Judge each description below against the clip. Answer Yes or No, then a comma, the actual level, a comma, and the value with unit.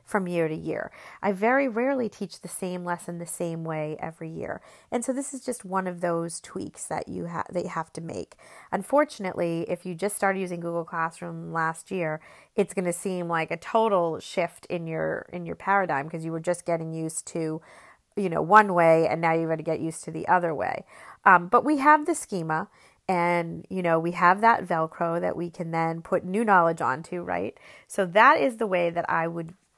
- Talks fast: Yes, fast, 220 wpm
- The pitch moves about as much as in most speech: Yes, average, 3.1 semitones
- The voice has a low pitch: No, medium, 175 Hz